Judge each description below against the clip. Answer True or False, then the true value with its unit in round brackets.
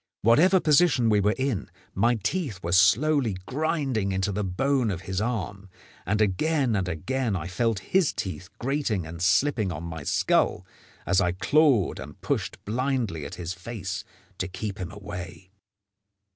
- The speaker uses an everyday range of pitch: False (6.2 semitones)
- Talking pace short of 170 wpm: True (160 wpm)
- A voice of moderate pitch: False (105 Hz)